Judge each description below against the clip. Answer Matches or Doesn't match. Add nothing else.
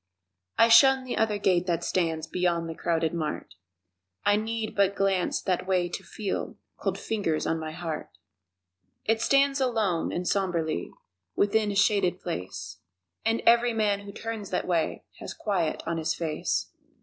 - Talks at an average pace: Matches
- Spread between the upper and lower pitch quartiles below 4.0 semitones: Doesn't match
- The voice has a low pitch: Doesn't match